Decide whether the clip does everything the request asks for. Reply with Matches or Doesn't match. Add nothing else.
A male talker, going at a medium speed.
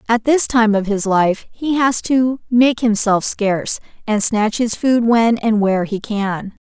Doesn't match